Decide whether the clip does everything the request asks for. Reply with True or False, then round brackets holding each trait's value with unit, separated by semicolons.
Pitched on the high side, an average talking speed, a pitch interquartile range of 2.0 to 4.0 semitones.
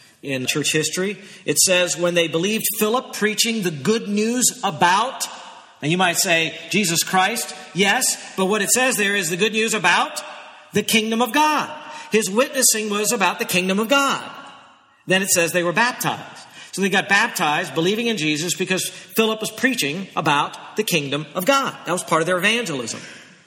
False (200 Hz; 180 wpm; 4.7 semitones)